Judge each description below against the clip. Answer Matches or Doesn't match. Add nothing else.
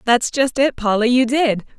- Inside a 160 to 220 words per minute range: Matches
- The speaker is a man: Doesn't match